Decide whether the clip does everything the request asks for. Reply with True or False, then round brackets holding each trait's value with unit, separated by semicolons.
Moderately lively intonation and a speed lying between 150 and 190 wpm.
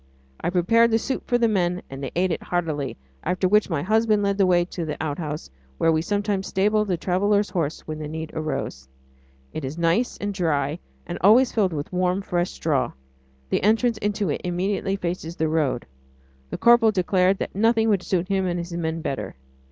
False (4.2 semitones; 200 wpm)